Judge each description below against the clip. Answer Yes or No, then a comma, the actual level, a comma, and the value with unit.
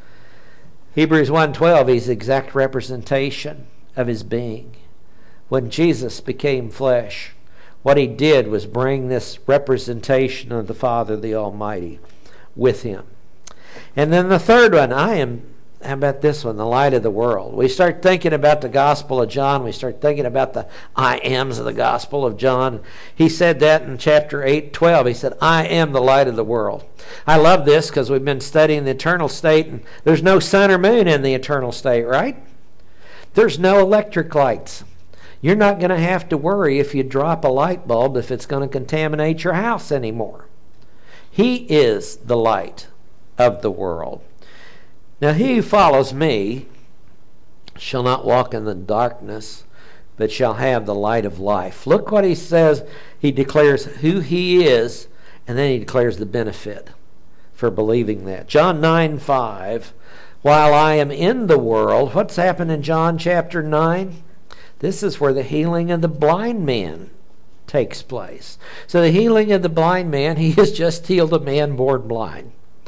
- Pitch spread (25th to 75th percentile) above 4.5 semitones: Yes, average, 5.3 semitones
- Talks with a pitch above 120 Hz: Yes, medium, 140 Hz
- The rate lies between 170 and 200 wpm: Yes, average, 175 wpm